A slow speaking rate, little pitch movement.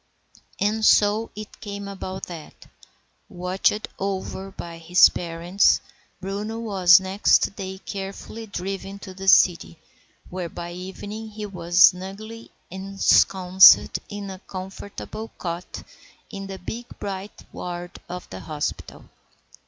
Yes: slow, 120 wpm; narrow, 2.1 semitones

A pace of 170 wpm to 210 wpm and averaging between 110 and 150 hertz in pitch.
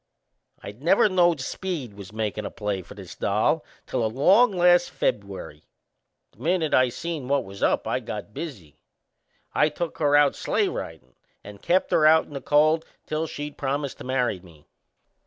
Yes: average, 175 wpm; medium, 140 Hz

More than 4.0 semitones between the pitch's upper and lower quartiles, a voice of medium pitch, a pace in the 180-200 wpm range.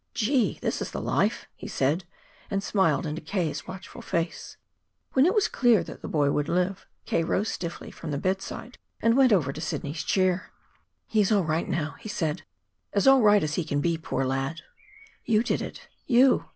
Yes: wide, 5.5 semitones; medium, 180 Hz; average, 190 wpm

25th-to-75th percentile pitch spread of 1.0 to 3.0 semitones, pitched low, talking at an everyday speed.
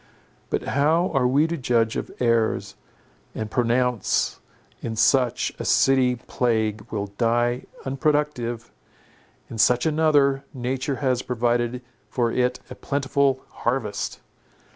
No: narrow, 2.6 semitones; low, 125 Hz; slow, 115 wpm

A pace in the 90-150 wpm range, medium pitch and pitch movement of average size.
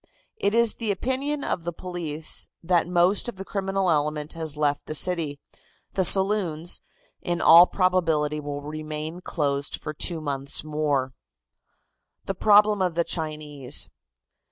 Yes: average, 140 wpm; medium, 170 Hz; average, 3.9 semitones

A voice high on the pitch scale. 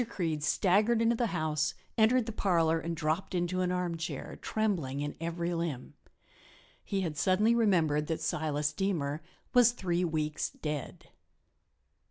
No: medium, 170 Hz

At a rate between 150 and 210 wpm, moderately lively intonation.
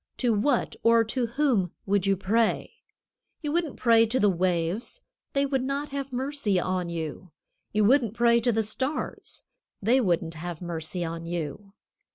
No: average, 165 wpm; wide, 6.4 semitones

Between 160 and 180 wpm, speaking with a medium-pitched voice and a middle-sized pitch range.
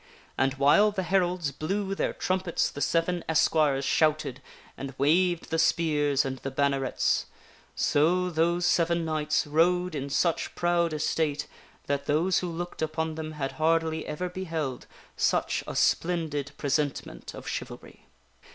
No: average, 140 wpm; medium, 160 Hz; average, 3.2 semitones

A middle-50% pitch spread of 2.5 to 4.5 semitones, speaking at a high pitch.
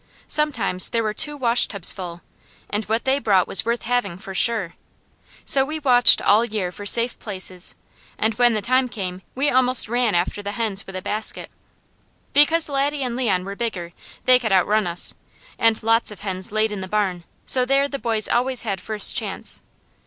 Yes: average, 4.2 semitones; high, 220 Hz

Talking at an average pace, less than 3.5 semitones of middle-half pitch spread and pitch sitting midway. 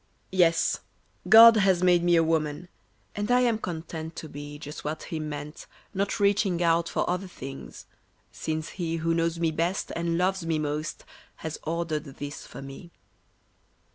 Yes: average, 165 wpm; average, 2.7 semitones; medium, 165 Hz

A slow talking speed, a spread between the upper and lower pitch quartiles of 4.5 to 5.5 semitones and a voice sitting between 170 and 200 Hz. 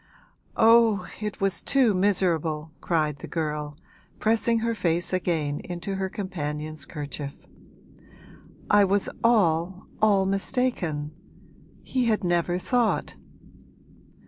Yes: slow, 105 wpm; average, 5.1 semitones; medium, 185 Hz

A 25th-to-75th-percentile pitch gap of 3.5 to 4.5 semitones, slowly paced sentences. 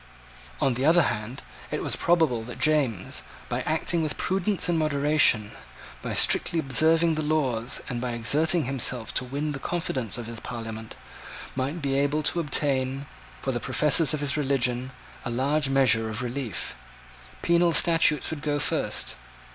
No: average, 4.0 semitones; average, 160 wpm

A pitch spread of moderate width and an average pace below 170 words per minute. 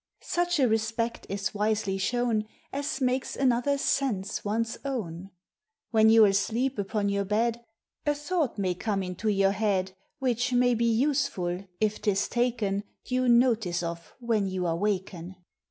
Yes: average, 4.0 semitones; average, 150 wpm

